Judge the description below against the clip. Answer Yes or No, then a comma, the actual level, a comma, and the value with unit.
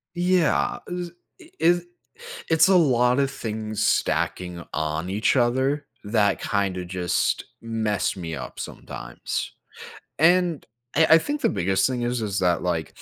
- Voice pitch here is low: Yes, low, 115 Hz